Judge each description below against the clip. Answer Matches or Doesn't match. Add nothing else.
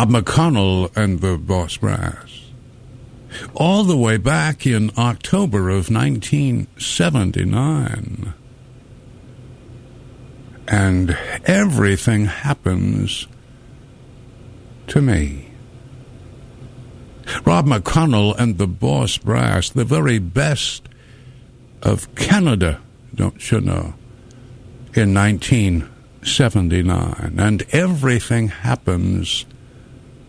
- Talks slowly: Matches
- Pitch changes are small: Doesn't match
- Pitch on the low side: Matches